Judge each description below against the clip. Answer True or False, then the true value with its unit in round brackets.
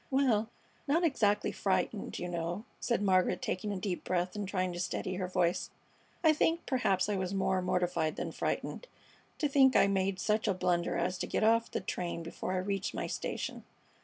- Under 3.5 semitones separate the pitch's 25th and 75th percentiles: True (3.1 semitones)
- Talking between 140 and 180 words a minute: False (190 wpm)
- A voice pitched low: False (190 Hz)